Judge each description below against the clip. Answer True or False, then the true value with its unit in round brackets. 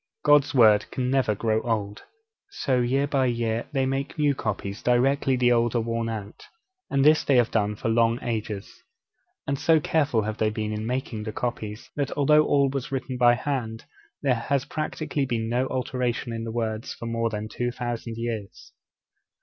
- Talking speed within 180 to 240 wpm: True (185 wpm)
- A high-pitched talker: False (120 Hz)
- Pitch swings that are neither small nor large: True (3.2 semitones)